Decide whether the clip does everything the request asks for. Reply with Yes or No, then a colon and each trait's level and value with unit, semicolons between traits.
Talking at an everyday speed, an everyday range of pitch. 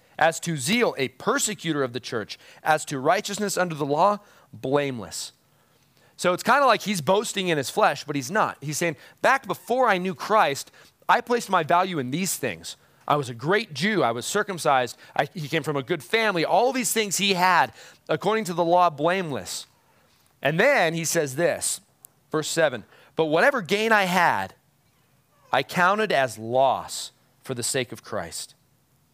No: average, 180 wpm; wide, 6.2 semitones